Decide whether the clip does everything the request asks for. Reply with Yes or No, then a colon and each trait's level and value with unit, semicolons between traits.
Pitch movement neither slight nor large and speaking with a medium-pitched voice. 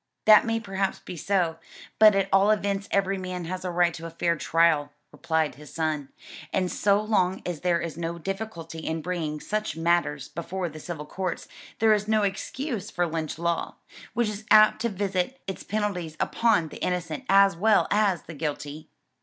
Yes: average, 3.7 semitones; medium, 180 Hz